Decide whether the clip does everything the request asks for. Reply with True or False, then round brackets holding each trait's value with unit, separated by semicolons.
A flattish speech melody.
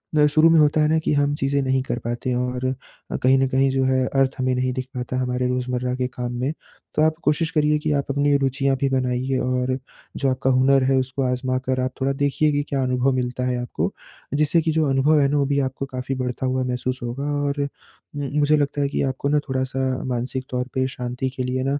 True (1.9 semitones)